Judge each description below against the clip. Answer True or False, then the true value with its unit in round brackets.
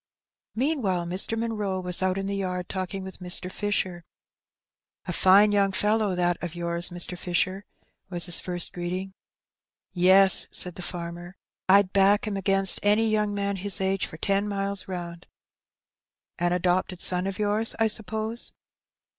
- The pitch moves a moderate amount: False (2.2 semitones)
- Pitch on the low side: False (190 Hz)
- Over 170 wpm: False (155 wpm)